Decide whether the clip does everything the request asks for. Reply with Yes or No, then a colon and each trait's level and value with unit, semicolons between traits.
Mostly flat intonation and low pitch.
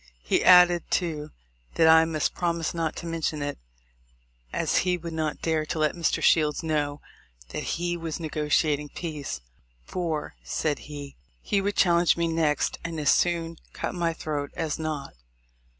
No: narrow, 2.1 semitones; medium, 160 Hz